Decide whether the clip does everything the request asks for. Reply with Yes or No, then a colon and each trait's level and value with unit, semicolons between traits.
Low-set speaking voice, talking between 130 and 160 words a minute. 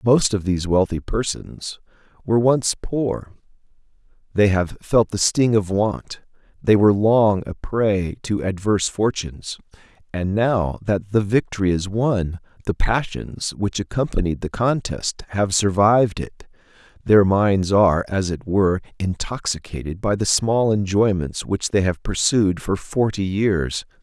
Yes: low, 100 Hz; average, 140 wpm